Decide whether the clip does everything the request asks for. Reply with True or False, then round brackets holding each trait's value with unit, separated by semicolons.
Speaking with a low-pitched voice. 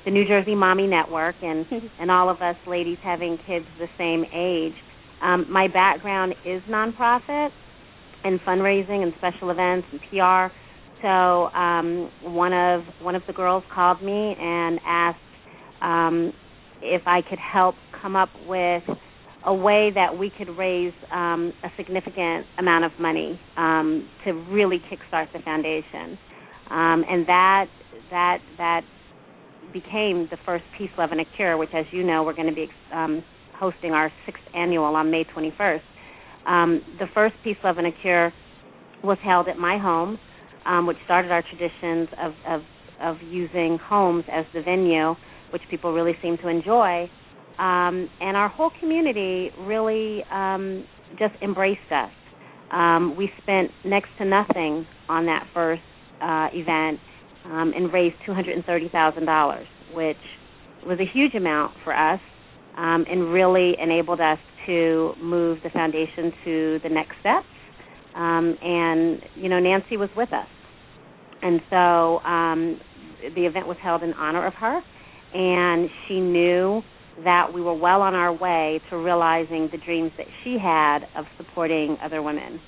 False (175 Hz)